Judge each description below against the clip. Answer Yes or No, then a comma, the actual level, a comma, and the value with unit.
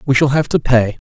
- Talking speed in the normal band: No, fast, 280 wpm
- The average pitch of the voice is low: Yes, low, 130 Hz